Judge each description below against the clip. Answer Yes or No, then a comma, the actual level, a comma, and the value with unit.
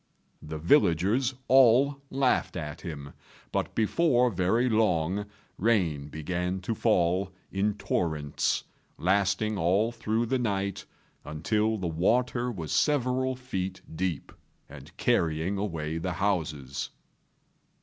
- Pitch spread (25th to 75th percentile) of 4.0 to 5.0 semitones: No, wide, 5.6 semitones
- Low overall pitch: Yes, very low, 95 Hz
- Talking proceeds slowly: Yes, slow, 110 wpm